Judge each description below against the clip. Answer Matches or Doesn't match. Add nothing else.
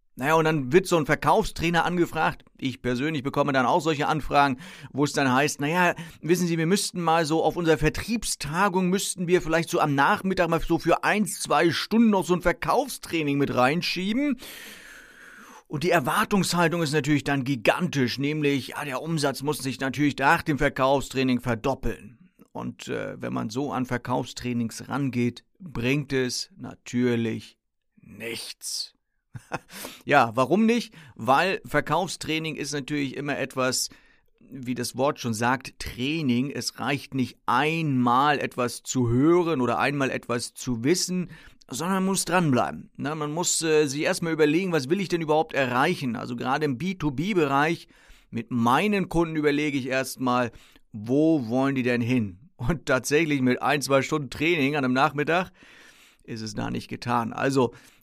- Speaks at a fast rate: Doesn't match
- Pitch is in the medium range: Matches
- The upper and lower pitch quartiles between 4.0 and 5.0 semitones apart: Matches